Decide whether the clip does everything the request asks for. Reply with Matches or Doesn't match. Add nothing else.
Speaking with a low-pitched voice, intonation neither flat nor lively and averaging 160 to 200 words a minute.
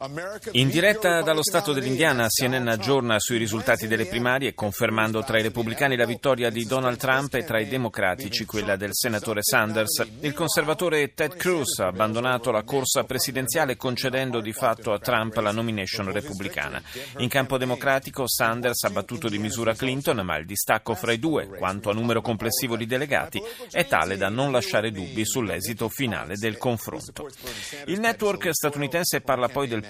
Matches